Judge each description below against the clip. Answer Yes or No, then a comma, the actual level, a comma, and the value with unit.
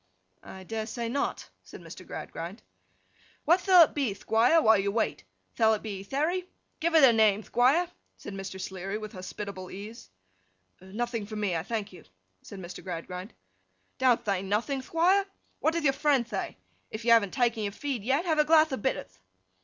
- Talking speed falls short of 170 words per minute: No, average, 185 wpm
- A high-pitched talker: Yes, high, 225 Hz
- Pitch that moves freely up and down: Yes, wide, 6.0 semitones